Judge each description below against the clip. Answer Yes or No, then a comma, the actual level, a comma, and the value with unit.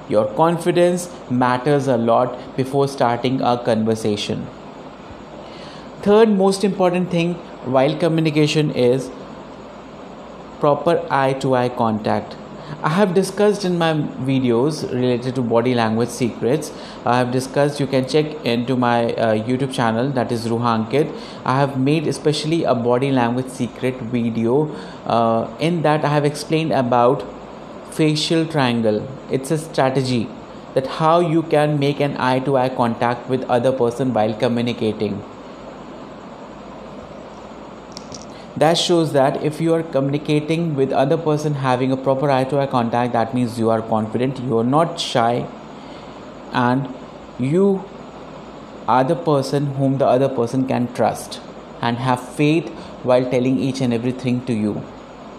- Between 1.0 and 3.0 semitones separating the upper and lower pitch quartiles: No, average, 3.9 semitones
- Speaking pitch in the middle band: No, low, 130 Hz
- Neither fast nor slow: Yes, average, 140 wpm